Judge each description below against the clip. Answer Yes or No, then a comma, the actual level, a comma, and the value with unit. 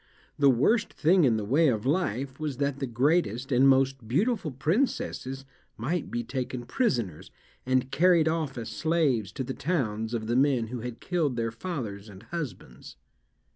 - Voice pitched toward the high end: No, low, 130 Hz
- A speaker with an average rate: Yes, average, 170 wpm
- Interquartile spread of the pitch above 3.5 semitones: Yes, average, 5.1 semitones